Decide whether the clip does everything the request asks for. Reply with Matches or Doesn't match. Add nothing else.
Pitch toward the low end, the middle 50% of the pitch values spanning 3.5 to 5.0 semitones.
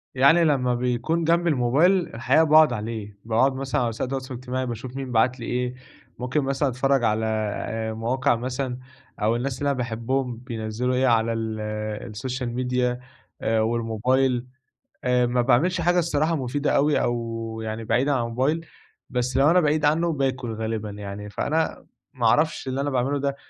Doesn't match